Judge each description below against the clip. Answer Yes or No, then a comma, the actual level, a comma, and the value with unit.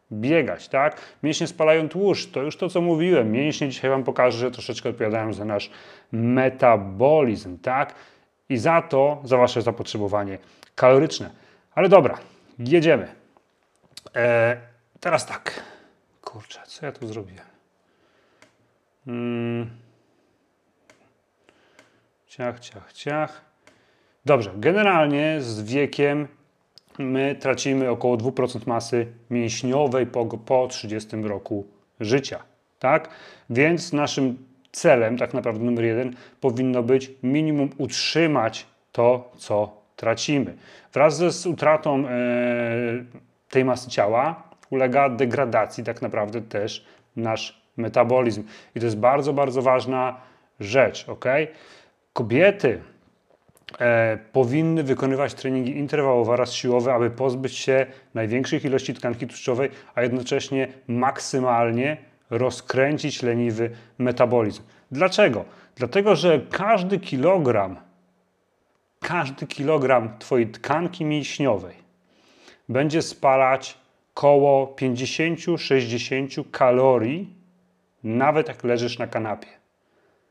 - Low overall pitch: Yes, low, 130 Hz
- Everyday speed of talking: No, slow, 100 wpm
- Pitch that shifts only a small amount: No, average, 3.3 semitones